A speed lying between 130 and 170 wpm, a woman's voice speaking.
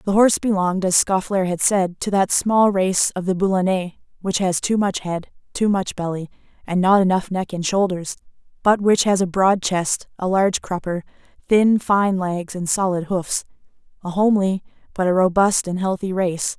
No: average, 180 wpm; female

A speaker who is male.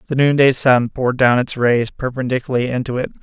Yes: male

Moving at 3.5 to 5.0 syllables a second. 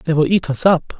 No: 5.3 syllables/s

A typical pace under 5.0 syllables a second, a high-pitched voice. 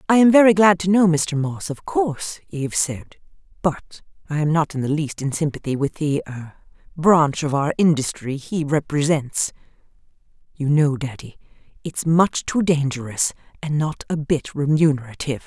No: 4.8 syllables/s; medium, 155 Hz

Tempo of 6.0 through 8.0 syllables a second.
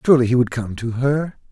Yes: 6.2 syllables/s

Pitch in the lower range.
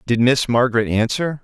Yes: low, 120 Hz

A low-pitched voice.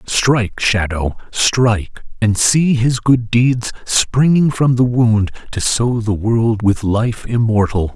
Yes: low, 115 Hz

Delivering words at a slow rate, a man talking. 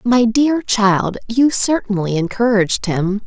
No: slow, 130 wpm; female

